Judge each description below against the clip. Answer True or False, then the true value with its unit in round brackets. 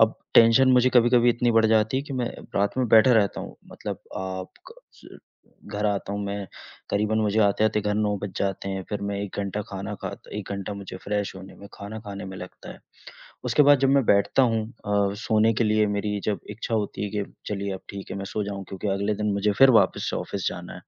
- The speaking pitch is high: False (105 Hz)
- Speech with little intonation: True (2.0 semitones)